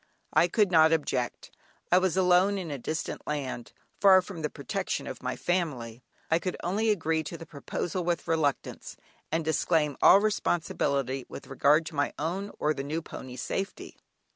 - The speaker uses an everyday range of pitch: Yes, average, 4.0 semitones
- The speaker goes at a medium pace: Yes, average, 170 wpm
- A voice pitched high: No, medium, 160 Hz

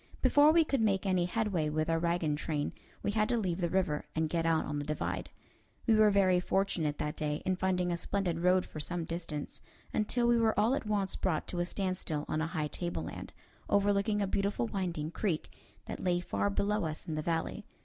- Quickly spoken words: Yes, fast, 210 wpm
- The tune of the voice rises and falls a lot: No, average, 4.0 semitones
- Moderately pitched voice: Yes, medium, 180 Hz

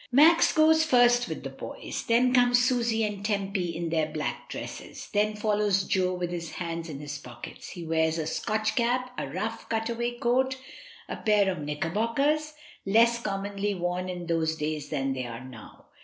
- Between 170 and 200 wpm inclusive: Yes, average, 185 wpm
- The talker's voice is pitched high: Yes, high, 200 Hz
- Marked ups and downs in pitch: Yes, wide, 6.4 semitones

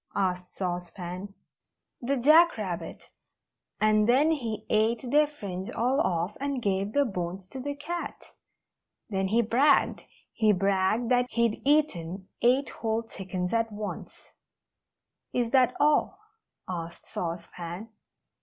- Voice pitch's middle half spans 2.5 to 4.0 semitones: No, wide, 5.5 semitones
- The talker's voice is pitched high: Yes, high, 215 Hz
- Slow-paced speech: Yes, slow, 130 wpm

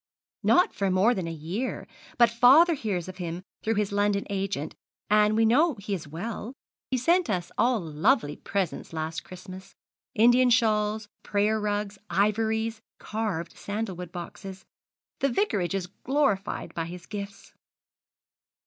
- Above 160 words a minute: No, average, 140 wpm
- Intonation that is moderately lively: Yes, average, 3.7 semitones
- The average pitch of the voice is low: No, high, 205 Hz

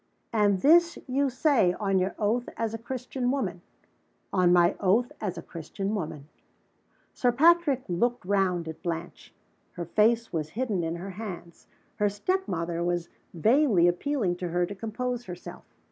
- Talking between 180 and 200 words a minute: No, average, 160 wpm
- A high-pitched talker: Yes, high, 200 Hz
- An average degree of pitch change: No, wide, 5.8 semitones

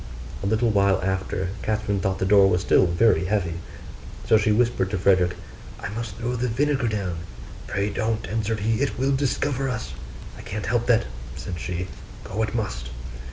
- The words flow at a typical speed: Yes, average, 180 wpm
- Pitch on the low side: Yes, low, 105 Hz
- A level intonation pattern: No, average, 3.4 semitones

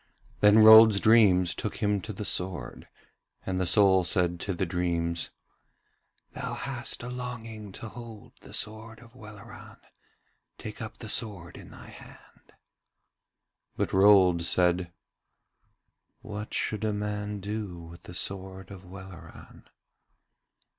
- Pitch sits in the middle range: No, low, 100 Hz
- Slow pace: Yes, slow, 130 wpm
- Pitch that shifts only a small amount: No, average, 3.2 semitones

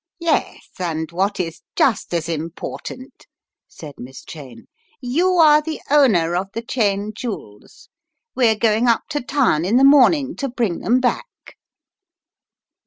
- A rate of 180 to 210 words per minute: No, average, 140 wpm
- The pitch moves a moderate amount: No, wide, 8.1 semitones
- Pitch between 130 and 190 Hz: No, high, 230 Hz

